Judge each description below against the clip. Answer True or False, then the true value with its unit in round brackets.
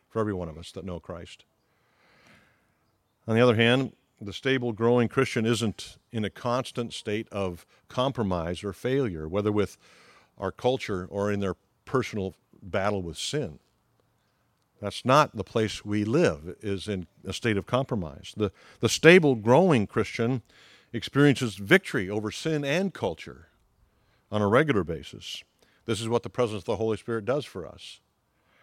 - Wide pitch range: False (3.6 semitones)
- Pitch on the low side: True (110 Hz)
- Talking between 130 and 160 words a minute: True (155 wpm)